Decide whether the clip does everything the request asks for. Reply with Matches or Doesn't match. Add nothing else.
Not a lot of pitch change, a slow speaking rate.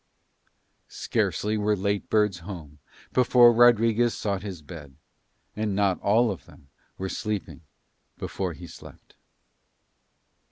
Doesn't match